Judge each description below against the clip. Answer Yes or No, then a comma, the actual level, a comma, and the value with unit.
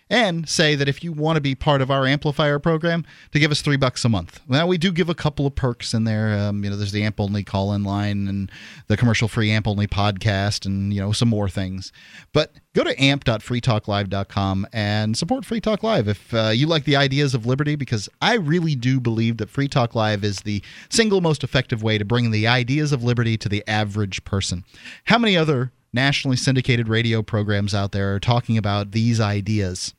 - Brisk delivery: Yes, fast, 220 wpm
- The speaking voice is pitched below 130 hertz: Yes, low, 115 Hz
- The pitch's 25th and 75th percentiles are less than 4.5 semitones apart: No, wide, 5.6 semitones